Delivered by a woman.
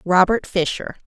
Yes: female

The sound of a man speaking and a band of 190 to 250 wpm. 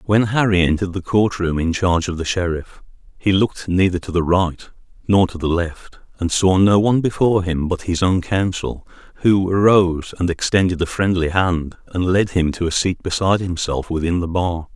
Yes: male; average, 200 wpm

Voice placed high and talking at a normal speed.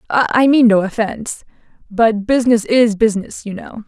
Yes: high, 225 Hz; average, 155 wpm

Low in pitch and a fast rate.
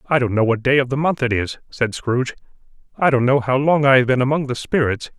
Yes: low, 130 Hz; fast, 265 wpm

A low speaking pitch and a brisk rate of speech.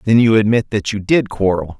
Yes: low, 105 Hz; fast, 235 wpm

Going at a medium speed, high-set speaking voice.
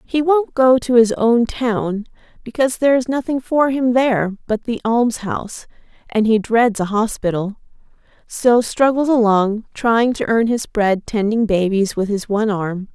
Yes: average, 165 wpm; high, 230 Hz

